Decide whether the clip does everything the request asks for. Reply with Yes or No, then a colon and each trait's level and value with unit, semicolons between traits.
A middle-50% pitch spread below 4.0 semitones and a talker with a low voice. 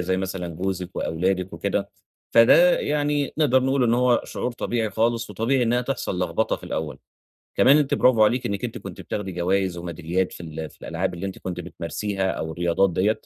No: average, 5.3 semitones; very low, 95 Hz